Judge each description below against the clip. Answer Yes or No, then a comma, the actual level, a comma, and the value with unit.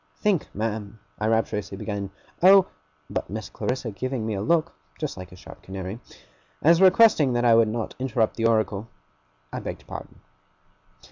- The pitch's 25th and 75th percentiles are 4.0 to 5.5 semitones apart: Yes, average, 4.4 semitones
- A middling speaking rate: Yes, average, 165 wpm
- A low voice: Yes, low, 110 Hz